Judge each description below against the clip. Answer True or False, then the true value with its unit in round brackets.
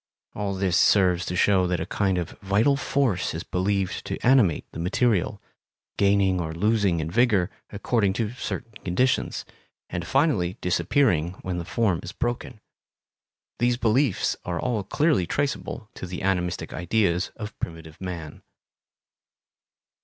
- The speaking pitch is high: False (95 Hz)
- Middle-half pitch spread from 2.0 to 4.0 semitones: False (4.5 semitones)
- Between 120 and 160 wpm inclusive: True (140 wpm)